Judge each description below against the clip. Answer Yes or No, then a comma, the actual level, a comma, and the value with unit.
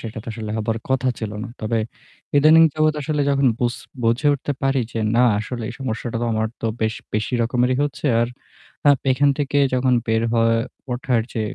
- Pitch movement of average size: Yes, average, 3.4 semitones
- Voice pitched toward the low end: Yes, low, 125 Hz